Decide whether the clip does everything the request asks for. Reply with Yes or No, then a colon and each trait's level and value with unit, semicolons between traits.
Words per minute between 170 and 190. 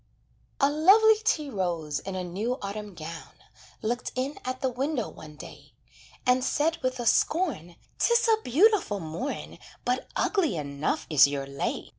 No: average, 155 wpm